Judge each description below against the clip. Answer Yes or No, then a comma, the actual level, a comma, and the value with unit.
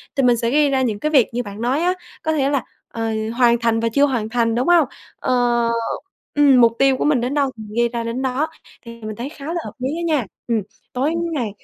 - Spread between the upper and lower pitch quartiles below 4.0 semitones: Yes, average, 3.3 semitones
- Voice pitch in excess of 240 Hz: Yes, very high, 250 Hz